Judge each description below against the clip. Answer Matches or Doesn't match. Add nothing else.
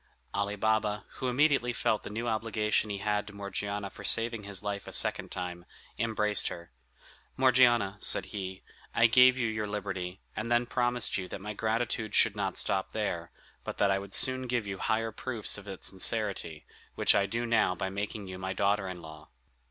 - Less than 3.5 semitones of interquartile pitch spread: Matches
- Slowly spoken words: Doesn't match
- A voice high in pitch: Doesn't match